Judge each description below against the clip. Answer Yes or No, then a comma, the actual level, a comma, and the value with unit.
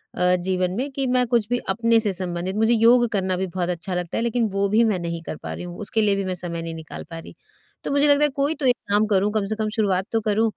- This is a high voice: Yes, high, 205 Hz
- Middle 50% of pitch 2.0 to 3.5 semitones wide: No, average, 4.2 semitones